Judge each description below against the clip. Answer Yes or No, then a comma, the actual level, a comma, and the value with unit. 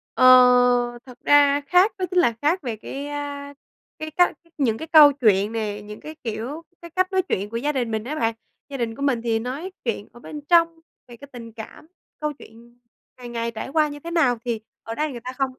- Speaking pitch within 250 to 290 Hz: Yes, very high, 270 Hz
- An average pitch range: Yes, average, 4.8 semitones